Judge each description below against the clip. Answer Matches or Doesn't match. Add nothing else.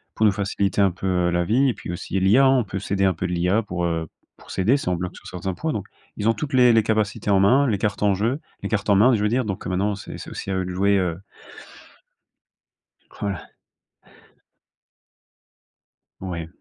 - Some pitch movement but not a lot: Matches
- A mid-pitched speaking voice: Doesn't match